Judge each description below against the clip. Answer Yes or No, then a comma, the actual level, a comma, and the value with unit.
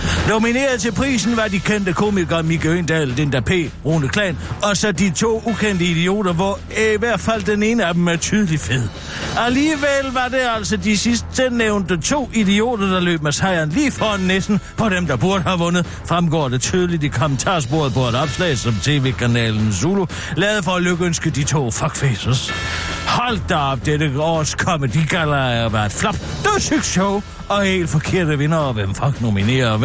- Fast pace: No, average, 185 wpm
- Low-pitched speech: No, medium, 175 Hz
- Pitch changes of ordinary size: No, wide, 6.6 semitones